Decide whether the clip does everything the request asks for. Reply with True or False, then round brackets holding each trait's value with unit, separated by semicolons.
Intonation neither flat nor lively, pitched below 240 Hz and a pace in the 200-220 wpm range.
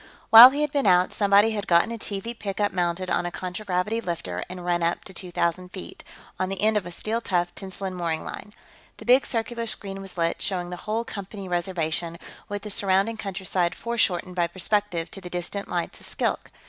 True (3.1 semitones; 190 Hz; 205 wpm)